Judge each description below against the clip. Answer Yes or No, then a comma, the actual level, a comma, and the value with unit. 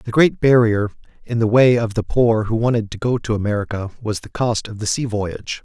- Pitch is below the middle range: Yes, low, 110 Hz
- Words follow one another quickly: Yes, fast, 235 wpm